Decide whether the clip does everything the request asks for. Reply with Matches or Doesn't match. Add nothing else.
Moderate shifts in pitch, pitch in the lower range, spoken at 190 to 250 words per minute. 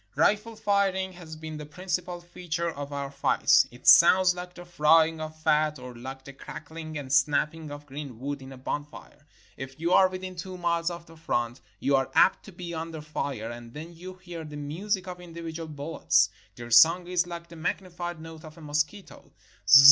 Doesn't match